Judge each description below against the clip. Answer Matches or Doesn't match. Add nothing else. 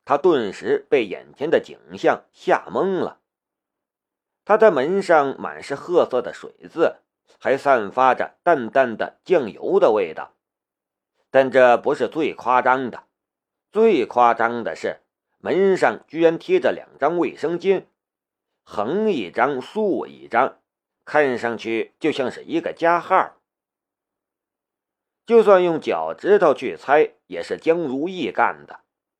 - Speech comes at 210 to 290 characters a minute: Doesn't match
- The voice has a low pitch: Doesn't match